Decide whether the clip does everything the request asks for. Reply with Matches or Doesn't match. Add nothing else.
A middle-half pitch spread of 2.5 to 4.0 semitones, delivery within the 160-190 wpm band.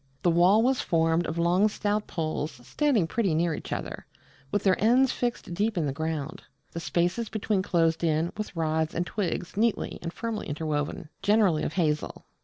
Doesn't match